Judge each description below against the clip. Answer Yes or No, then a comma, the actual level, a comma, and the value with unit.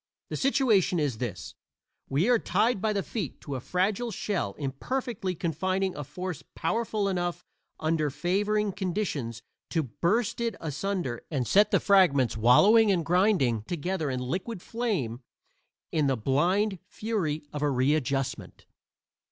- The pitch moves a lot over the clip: Yes, wide, 6.7 semitones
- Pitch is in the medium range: Yes, medium, 175 Hz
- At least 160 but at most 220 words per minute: No, average, 140 wpm